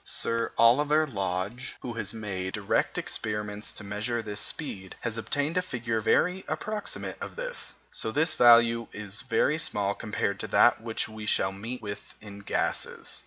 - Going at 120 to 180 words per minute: Yes, average, 160 wpm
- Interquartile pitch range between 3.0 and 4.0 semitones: Yes, average, 3.6 semitones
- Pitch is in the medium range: No, low, 115 Hz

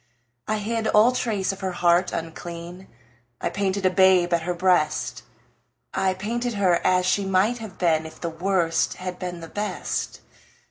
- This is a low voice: No, medium, 185 Hz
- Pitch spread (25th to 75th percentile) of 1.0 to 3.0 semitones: Yes, average, 2.7 semitones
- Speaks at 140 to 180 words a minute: Yes, average, 170 wpm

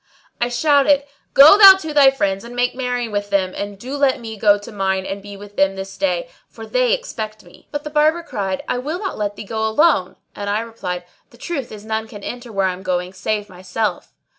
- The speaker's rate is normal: No, fast, 230 wpm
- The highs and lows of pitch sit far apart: Yes, wide, 6.0 semitones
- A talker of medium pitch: No, high, 220 Hz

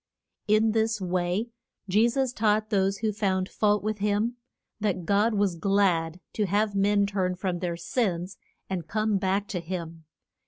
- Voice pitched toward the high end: Yes, high, 200 Hz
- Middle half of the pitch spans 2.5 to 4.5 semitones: Yes, average, 2.8 semitones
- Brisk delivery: No, average, 160 wpm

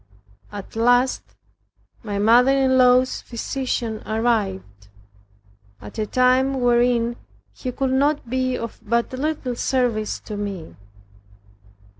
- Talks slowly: Yes, slow, 105 wpm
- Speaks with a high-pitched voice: Yes, high, 240 Hz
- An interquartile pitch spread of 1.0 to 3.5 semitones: Yes, average, 3.0 semitones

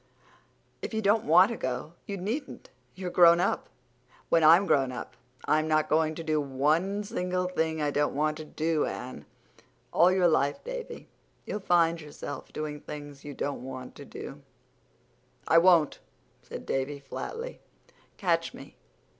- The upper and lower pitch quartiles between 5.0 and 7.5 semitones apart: No, average, 3.9 semitones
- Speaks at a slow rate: No, average, 155 wpm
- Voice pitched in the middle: Yes, medium, 160 Hz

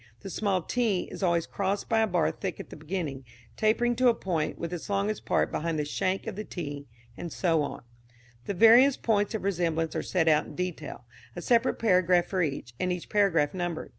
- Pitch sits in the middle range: Yes, medium, 180 Hz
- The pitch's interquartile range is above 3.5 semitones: Yes, average, 4.0 semitones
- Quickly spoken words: Yes, fast, 210 wpm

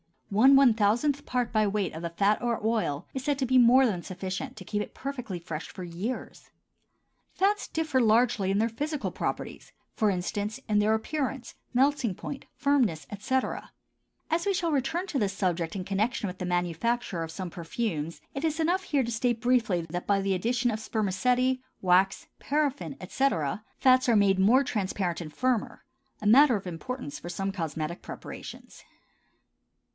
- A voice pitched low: No, high, 220 Hz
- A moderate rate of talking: Yes, average, 170 wpm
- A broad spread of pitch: Yes, wide, 5.7 semitones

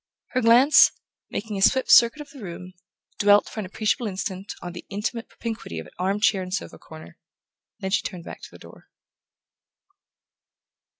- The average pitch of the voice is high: Yes, high, 205 Hz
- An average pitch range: Yes, average, 4.0 semitones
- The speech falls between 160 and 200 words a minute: Yes, average, 170 wpm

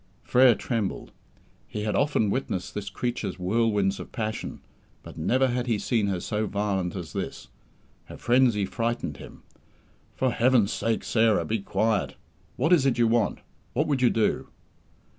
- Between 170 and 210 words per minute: No, average, 160 wpm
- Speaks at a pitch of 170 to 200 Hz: No, low, 115 Hz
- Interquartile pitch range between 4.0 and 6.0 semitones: No, average, 3.4 semitones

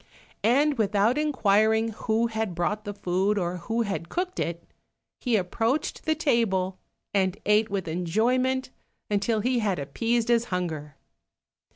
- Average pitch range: Yes, average, 4.1 semitones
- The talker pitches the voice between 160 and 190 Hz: No, high, 215 Hz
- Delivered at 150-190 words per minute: No, average, 140 wpm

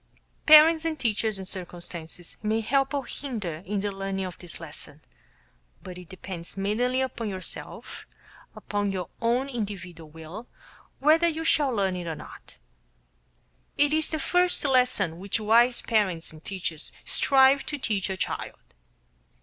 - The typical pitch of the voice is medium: No, high, 205 Hz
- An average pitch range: No, wide, 6.6 semitones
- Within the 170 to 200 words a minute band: No, average, 150 wpm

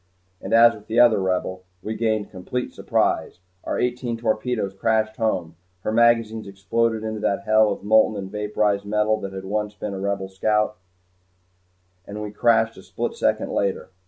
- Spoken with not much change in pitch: Yes, narrow, 2.0 semitones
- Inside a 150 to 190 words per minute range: Yes, average, 170 wpm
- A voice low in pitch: Yes, low, 105 Hz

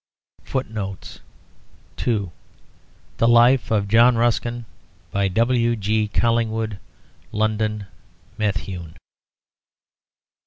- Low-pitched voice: Yes, low, 110 Hz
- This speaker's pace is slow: Yes, slow, 65 wpm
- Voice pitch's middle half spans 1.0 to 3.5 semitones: Yes, narrow, 2.4 semitones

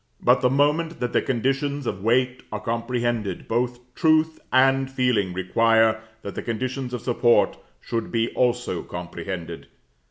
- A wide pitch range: No, average, 2.9 semitones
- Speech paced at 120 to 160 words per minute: Yes, average, 145 wpm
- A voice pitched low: Yes, low, 120 Hz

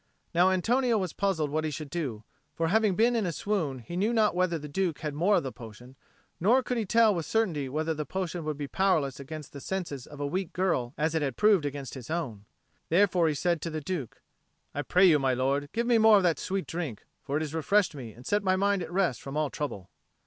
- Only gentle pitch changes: No, average, 5.1 semitones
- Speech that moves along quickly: Yes, fast, 245 wpm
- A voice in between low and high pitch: Yes, medium, 165 Hz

